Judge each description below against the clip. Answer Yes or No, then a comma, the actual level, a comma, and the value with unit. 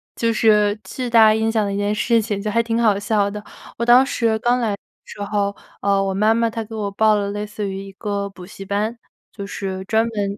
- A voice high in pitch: Yes, high, 210 Hz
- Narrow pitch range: Yes, narrow, 2.0 semitones